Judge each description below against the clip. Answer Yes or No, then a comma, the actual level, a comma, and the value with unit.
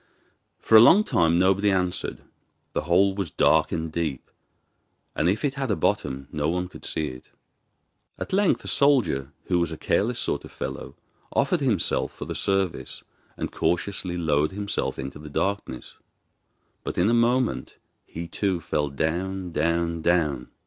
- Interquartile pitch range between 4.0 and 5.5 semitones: Yes, average, 4.3 semitones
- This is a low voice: Yes, very low, 90 Hz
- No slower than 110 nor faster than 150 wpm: No, average, 165 wpm